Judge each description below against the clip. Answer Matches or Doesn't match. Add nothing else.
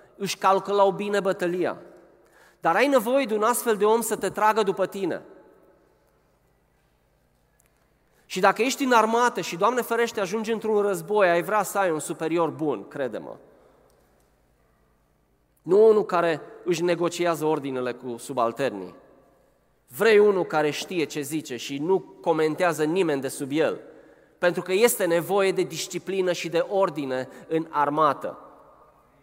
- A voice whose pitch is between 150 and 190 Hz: Matches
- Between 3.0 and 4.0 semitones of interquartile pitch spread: Doesn't match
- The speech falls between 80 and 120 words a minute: Doesn't match